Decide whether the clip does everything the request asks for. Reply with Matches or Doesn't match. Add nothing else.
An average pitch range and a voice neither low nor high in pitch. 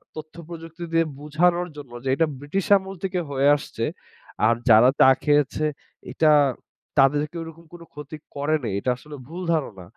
Matches